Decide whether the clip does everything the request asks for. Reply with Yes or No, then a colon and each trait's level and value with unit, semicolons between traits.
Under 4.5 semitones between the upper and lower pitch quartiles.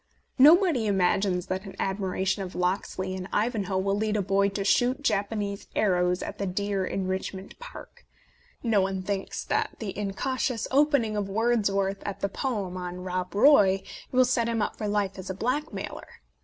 Yes: average, 2.9 semitones